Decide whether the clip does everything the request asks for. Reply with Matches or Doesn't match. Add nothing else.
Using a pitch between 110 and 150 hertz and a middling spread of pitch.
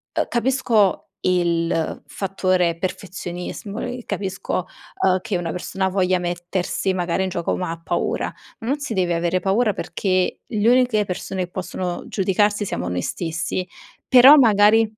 Doesn't match